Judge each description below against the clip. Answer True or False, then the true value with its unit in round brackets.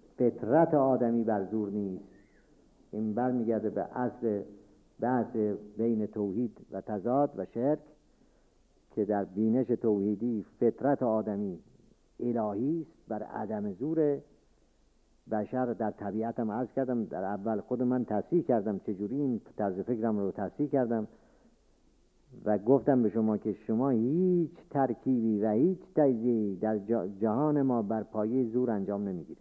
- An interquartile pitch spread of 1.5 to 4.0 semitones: True (3.3 semitones)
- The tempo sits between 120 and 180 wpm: True (130 wpm)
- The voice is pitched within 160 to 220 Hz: False (115 Hz)